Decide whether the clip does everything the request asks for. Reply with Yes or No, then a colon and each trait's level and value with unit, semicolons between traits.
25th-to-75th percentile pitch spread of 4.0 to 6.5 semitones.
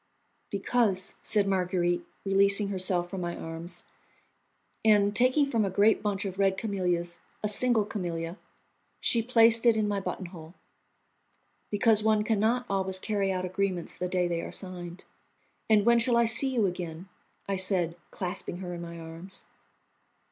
No: average, 3.3 semitones